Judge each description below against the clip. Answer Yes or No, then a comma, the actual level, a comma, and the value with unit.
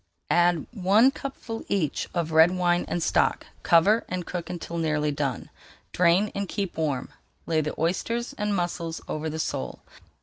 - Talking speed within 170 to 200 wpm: No, average, 160 wpm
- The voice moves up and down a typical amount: Yes, average, 3.6 semitones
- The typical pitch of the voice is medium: Yes, medium, 175 Hz